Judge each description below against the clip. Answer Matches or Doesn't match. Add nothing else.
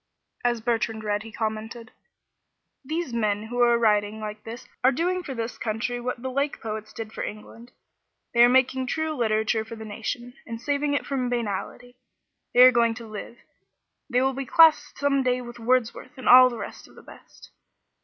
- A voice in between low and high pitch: Doesn't match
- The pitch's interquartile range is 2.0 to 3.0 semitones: Matches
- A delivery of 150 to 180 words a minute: Doesn't match